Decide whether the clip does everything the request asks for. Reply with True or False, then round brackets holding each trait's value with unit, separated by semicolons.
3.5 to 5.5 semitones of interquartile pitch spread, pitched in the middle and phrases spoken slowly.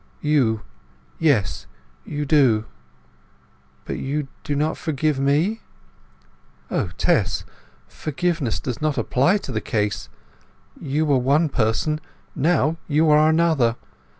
True (4.6 semitones; 145 Hz; 110 wpm)